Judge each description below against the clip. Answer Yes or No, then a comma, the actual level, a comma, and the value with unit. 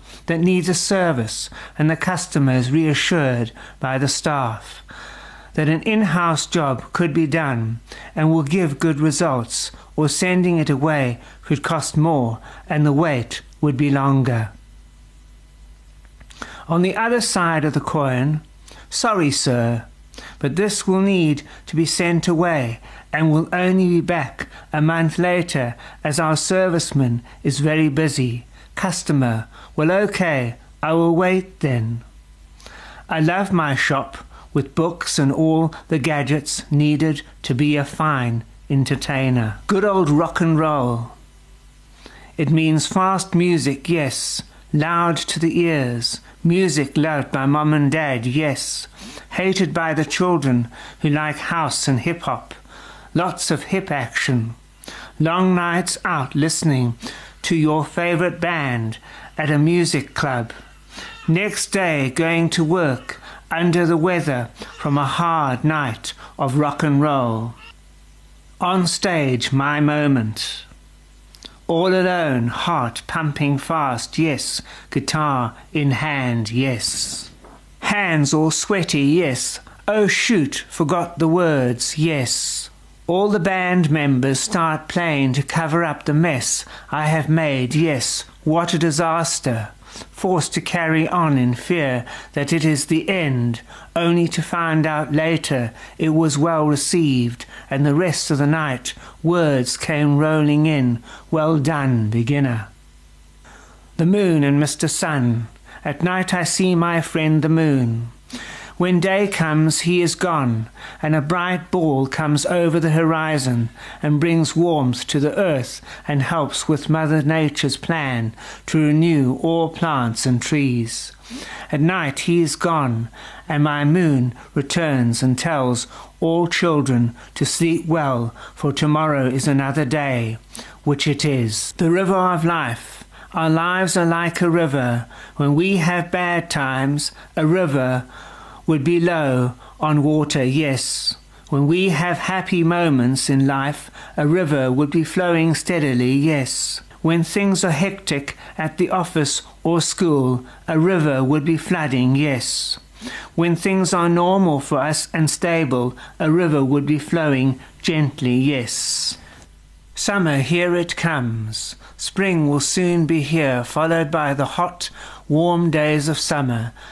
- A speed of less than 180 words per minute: Yes, average, 140 wpm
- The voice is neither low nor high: Yes, medium, 155 Hz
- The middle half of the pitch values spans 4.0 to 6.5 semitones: Yes, average, 4.3 semitones